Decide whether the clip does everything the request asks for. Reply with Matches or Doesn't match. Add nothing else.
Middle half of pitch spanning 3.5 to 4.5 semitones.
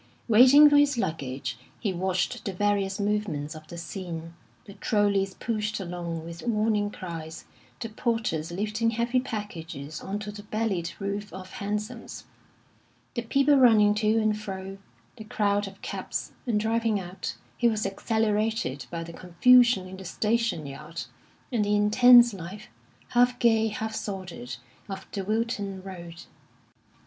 Matches